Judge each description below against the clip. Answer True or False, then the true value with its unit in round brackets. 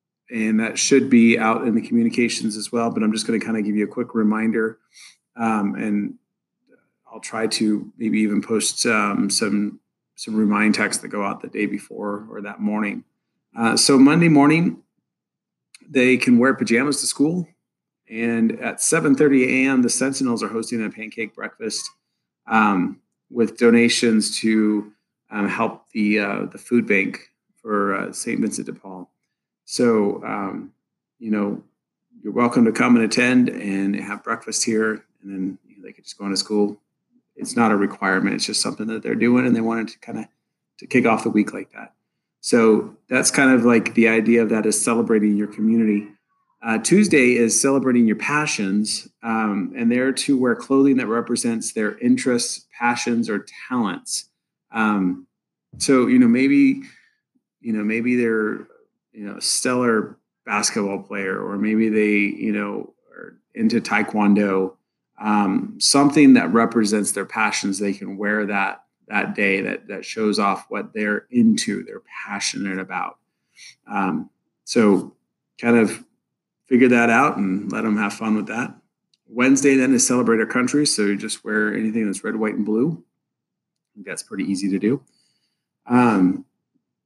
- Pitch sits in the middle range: False (115 Hz)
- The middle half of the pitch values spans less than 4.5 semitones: True (3.0 semitones)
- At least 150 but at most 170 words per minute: True (165 wpm)